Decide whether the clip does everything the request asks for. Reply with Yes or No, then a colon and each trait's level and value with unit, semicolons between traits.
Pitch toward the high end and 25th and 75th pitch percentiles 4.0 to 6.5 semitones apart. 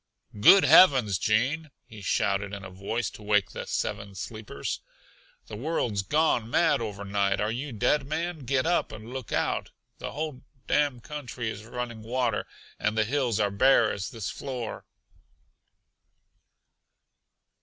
No: low, 115 Hz; average, 4.7 semitones